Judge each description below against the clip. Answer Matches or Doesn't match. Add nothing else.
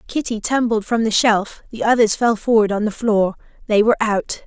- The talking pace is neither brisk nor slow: Matches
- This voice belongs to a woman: Matches